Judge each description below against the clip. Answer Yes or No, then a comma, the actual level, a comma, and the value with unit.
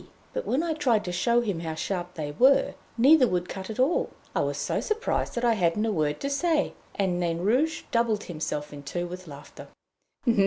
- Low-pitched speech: No, high, 205 Hz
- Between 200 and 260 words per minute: Yes, fast, 205 wpm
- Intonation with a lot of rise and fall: Yes, wide, 6.7 semitones